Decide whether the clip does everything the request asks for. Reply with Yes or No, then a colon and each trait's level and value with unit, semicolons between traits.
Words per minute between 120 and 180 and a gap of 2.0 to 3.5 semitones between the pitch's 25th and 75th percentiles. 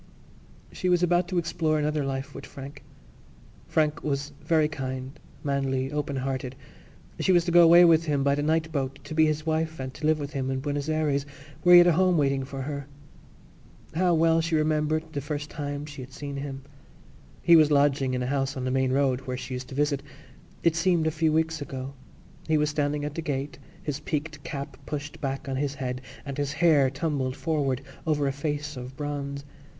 No: fast, 205 wpm; narrow, 2.5 semitones